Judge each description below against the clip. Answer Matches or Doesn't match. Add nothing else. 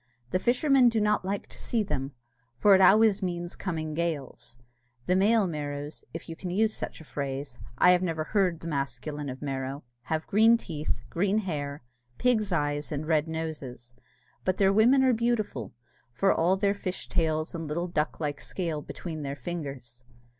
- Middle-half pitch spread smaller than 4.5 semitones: Doesn't match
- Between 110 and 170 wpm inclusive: Doesn't match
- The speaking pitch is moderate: Matches